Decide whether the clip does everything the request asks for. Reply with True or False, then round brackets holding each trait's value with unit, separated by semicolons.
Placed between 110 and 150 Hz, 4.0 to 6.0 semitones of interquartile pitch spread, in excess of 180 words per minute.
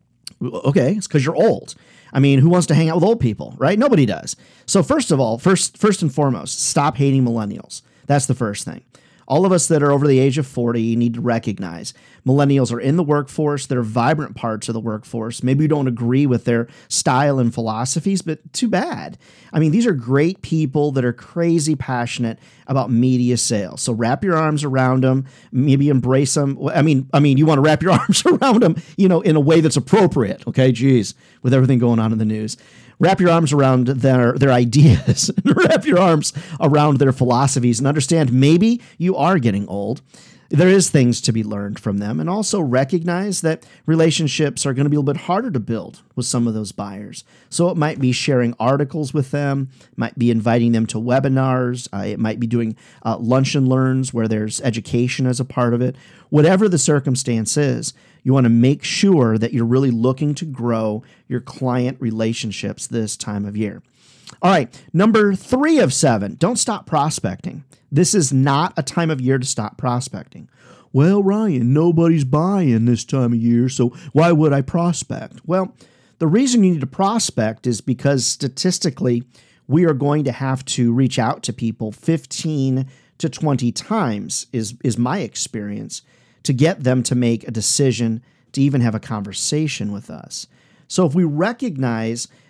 True (135 Hz; 4.8 semitones; 195 wpm)